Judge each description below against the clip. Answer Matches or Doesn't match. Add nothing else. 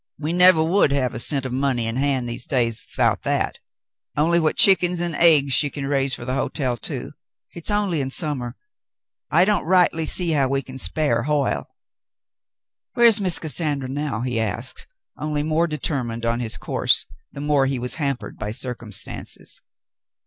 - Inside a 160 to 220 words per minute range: Matches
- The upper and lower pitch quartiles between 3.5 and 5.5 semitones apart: Matches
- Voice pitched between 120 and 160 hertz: Matches